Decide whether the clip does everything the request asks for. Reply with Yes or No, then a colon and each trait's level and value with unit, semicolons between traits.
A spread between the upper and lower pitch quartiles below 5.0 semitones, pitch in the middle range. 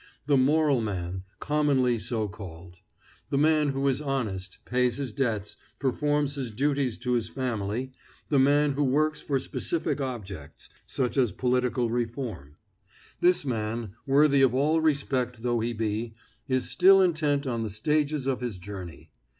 No: average, 4.4 semitones; low, 125 Hz